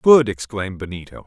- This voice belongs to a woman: No, male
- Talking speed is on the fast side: No, average, 145 wpm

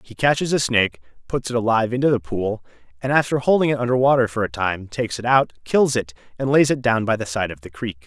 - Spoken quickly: Yes, fast, 255 wpm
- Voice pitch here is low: Yes, low, 120 Hz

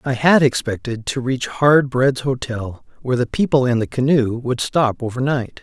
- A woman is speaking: No, male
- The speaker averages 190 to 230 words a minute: No, average, 180 wpm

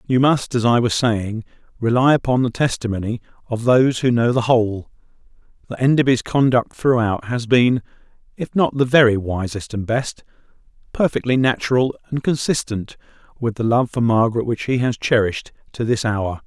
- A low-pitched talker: Yes, low, 120 Hz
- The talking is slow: No, average, 165 wpm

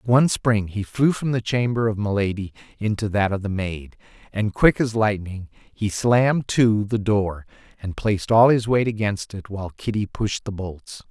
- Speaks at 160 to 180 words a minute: No, average, 195 wpm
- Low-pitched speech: Yes, low, 105 Hz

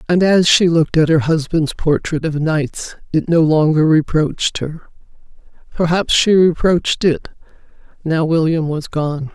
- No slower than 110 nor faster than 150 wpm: Yes, average, 140 wpm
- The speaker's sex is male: No, female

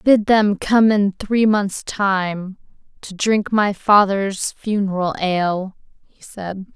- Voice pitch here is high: Yes, high, 200 Hz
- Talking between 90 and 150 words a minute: Yes, slow, 135 wpm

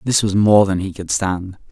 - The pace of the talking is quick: Yes, fast, 245 wpm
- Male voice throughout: Yes, male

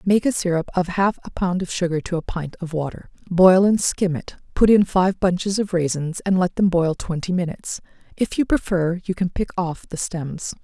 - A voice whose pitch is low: No, medium, 180 Hz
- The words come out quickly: Yes, fast, 220 wpm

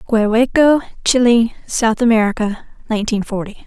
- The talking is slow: Yes, slow, 100 wpm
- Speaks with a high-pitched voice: Yes, high, 225 Hz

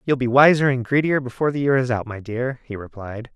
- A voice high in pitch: No, low, 125 Hz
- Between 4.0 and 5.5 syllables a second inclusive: No, 6.0 syllables/s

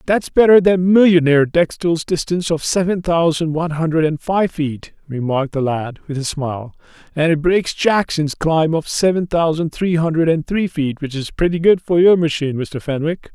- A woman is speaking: No, male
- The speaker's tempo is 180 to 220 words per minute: Yes, average, 190 wpm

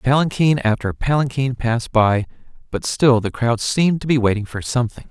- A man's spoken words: Yes, male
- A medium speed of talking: Yes, average, 175 wpm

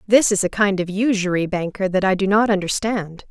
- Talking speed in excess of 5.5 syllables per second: No, 5.4 syllables/s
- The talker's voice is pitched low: No, high, 195 Hz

